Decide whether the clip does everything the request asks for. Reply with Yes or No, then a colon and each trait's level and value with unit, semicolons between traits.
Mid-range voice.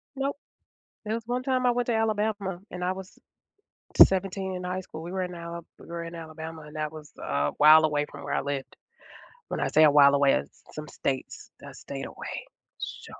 Yes: medium, 170 Hz